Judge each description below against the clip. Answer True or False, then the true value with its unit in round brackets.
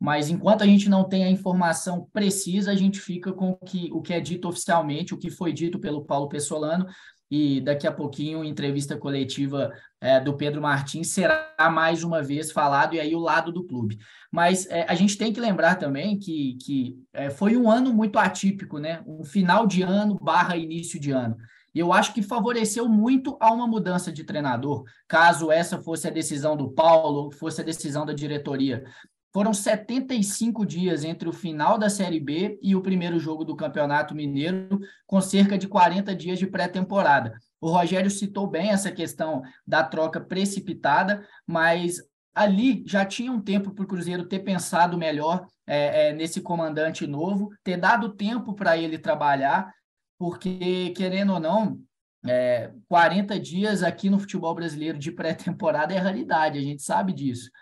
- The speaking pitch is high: False (175 Hz)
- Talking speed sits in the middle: True (175 wpm)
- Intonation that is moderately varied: True (4.0 semitones)